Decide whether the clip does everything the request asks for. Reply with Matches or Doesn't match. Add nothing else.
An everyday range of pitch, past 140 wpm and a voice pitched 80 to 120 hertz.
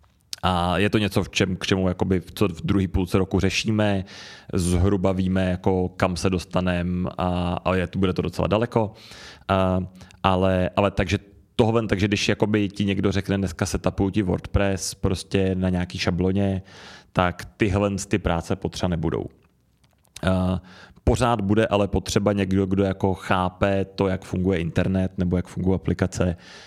Doesn't match